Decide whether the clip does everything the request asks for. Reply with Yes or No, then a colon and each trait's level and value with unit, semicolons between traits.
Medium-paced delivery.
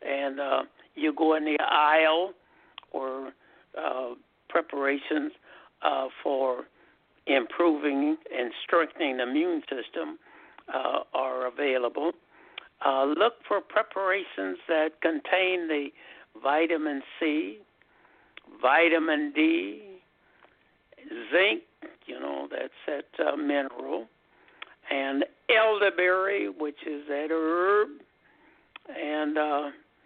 No: slow, 95 wpm